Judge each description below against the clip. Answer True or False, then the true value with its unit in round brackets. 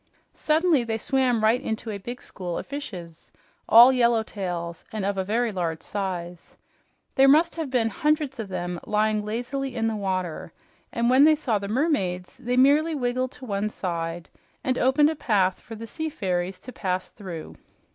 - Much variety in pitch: True (5.8 semitones)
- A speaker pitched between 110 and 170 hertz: False (225 Hz)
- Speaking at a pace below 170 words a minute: False (175 wpm)